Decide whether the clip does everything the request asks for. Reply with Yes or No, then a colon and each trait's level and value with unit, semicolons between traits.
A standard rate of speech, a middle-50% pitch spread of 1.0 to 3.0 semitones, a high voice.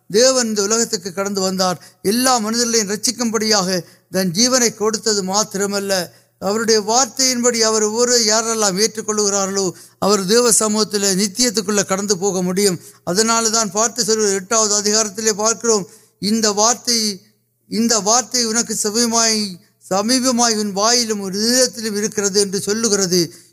No: slow, 65 wpm; narrow, 2.4 semitones; high, 215 Hz